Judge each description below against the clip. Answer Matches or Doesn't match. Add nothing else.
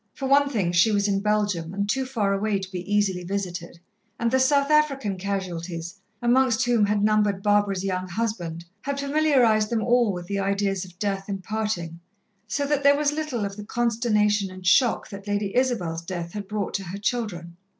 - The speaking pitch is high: Matches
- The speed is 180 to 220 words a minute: Matches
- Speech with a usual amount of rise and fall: Matches